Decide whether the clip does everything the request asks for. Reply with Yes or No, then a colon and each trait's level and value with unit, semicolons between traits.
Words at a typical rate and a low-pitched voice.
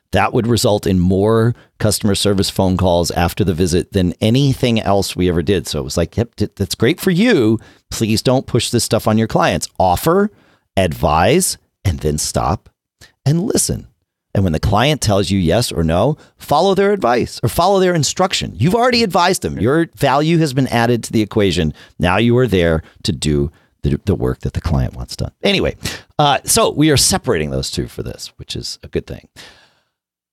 Yes: average, 195 wpm; low, 105 Hz